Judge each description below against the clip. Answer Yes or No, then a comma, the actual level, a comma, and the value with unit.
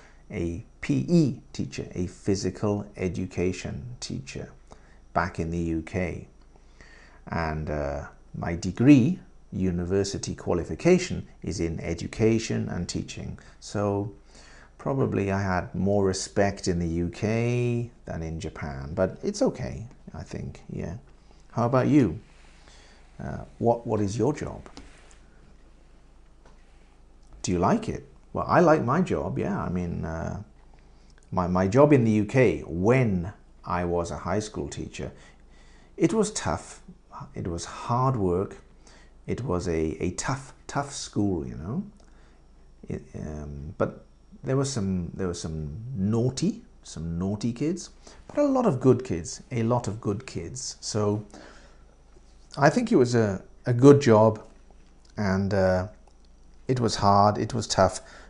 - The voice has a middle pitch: No, low, 100 Hz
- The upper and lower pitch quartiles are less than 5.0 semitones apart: No, wide, 5.6 semitones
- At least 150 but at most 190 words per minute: No, slow, 135 wpm